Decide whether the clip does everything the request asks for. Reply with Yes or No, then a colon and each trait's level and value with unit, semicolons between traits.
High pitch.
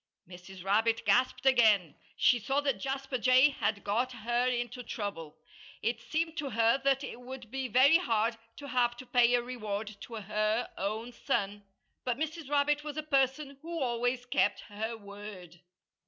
Yes: high, 245 Hz